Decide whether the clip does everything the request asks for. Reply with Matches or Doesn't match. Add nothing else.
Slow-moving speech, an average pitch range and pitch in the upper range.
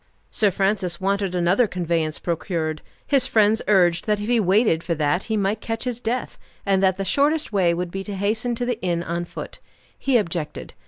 Doesn't match